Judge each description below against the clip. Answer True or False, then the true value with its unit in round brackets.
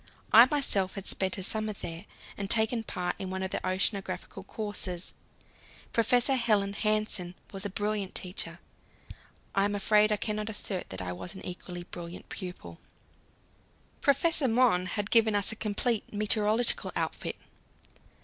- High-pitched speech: True (205 Hz)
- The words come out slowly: False (150 wpm)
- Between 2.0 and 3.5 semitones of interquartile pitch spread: True (2.9 semitones)